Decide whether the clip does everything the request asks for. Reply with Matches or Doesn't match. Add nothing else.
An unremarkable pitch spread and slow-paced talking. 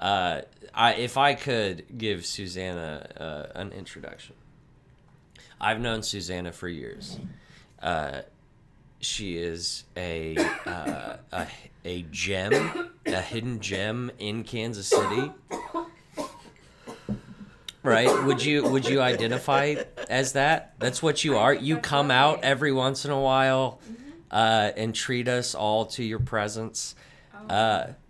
Matches